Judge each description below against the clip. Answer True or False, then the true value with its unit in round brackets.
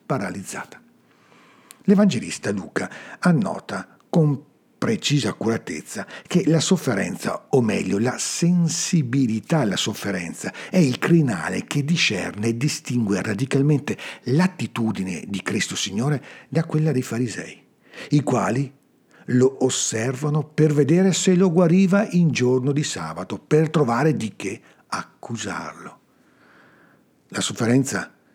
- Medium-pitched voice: True (145 Hz)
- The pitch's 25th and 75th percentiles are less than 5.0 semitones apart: False (5.3 semitones)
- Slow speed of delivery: True (110 wpm)